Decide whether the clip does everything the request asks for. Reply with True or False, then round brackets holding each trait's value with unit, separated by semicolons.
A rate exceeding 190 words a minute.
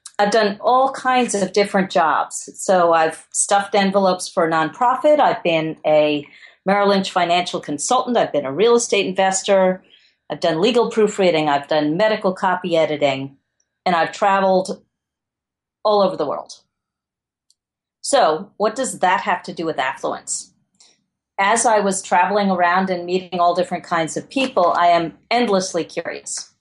False (155 wpm)